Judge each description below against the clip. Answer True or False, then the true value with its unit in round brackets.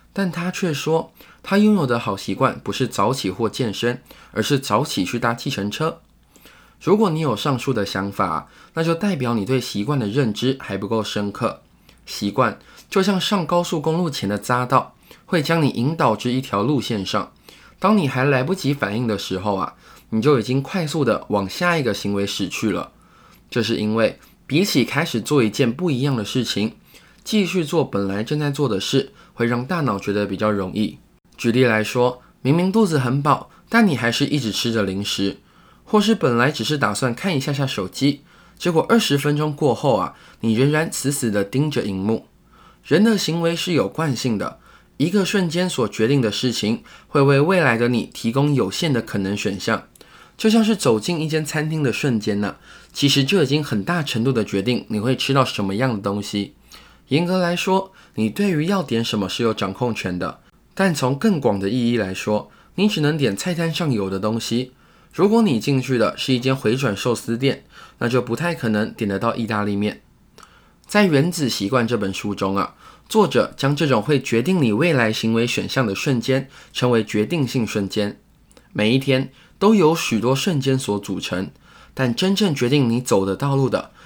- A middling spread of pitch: False (6.6 semitones)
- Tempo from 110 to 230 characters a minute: False (275 characters per minute)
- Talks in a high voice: False (130 Hz)